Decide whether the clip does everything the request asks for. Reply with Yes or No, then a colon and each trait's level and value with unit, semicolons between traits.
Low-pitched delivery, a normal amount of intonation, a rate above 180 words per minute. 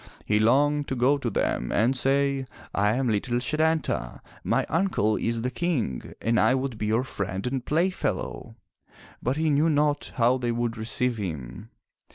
No: low, 125 Hz; average, 4.5 semitones; average, 170 wpm